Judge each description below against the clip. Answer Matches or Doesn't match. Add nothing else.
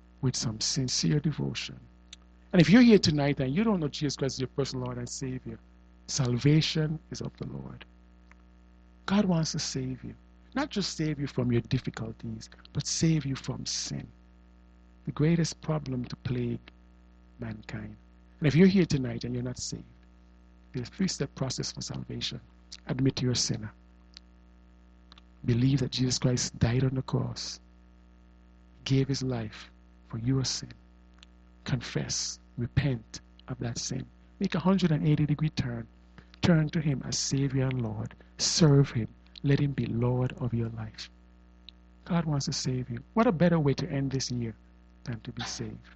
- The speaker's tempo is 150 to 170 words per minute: Matches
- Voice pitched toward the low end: Matches